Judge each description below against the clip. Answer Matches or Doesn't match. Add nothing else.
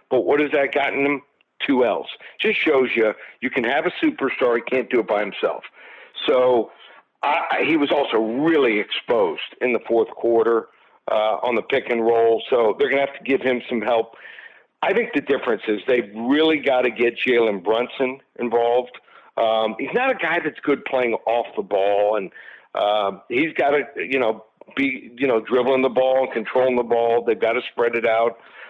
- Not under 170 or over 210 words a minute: Matches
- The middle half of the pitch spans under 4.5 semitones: Doesn't match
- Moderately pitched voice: Doesn't match